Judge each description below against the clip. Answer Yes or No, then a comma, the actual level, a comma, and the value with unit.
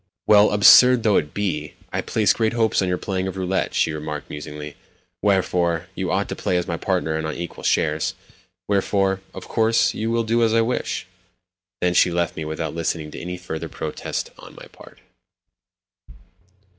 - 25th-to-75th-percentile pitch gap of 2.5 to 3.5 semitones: No, average, 4.7 semitones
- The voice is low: Yes, very low, 90 Hz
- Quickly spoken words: No, average, 180 wpm